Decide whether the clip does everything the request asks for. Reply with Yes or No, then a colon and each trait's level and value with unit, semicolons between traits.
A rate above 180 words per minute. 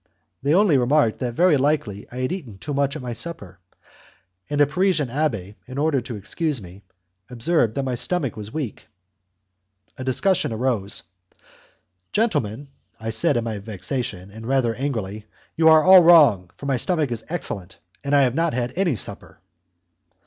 No: average, 170 wpm